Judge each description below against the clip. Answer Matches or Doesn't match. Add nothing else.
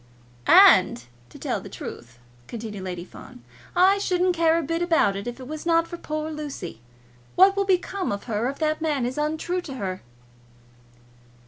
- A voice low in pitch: Doesn't match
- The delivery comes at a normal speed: Matches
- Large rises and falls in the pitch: Matches